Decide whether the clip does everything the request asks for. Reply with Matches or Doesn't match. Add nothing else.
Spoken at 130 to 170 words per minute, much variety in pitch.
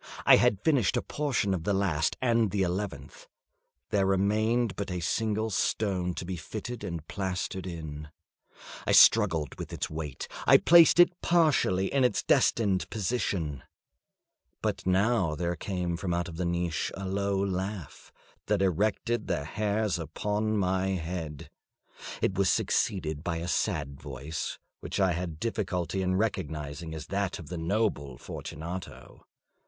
Doesn't match